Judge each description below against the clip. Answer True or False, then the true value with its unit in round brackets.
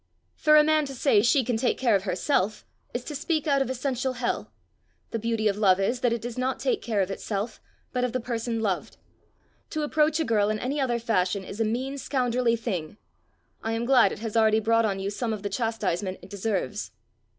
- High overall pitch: True (230 Hz)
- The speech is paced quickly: True (220 wpm)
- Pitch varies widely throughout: False (3.8 semitones)